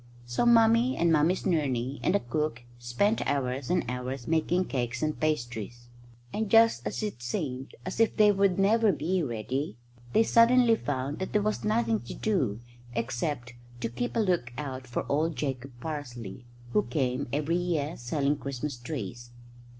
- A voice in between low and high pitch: Yes, medium, 150 Hz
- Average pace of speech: Yes, average, 160 wpm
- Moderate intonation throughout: No, wide, 7.7 semitones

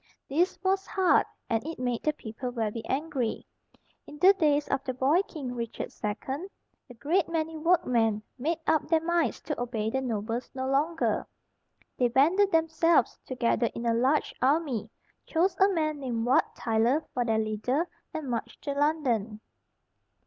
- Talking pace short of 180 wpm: Yes, average, 160 wpm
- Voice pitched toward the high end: Yes, very high, 270 Hz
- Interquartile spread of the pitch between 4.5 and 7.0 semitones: Yes, wide, 5.4 semitones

